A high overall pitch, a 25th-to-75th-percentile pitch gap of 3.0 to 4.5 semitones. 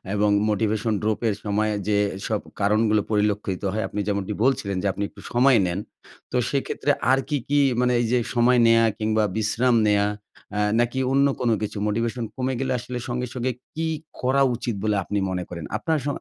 No: low, 110 Hz; average, 3.3 semitones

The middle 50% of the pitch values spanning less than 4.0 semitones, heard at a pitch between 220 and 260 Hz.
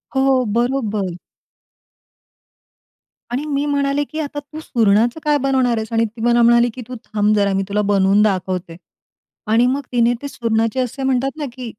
No: average, 4.3 semitones; high, 240 Hz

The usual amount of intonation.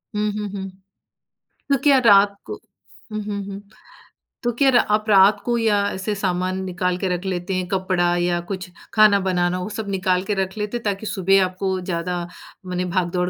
No: narrow, 2.3 semitones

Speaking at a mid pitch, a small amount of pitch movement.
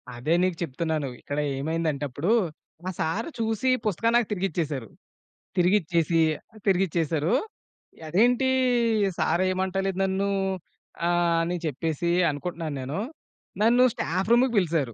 No: medium, 175 Hz; average, 3.7 semitones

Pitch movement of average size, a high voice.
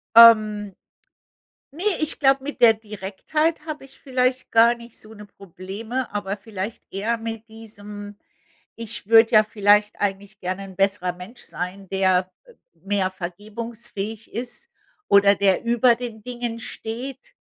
Yes: average, 3.0 semitones; high, 215 Hz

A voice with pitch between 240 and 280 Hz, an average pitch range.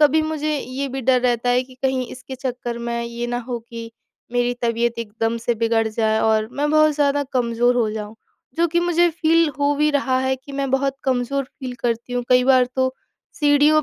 Yes: very high, 255 Hz; average, 3.3 semitones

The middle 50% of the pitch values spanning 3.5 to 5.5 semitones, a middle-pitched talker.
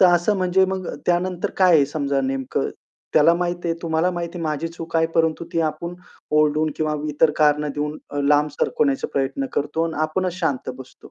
No: average, 2.8 semitones; medium, 160 Hz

